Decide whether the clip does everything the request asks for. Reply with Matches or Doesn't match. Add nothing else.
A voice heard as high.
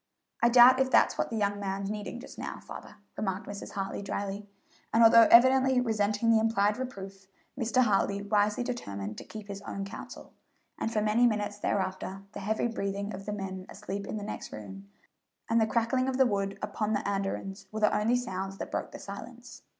Matches